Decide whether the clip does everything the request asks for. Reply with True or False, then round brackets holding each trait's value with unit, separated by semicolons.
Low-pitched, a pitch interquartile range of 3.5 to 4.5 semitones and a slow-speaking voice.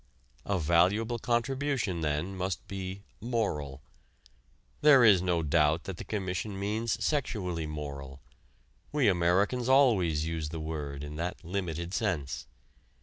False (90 Hz; 5.5 semitones; 125 wpm)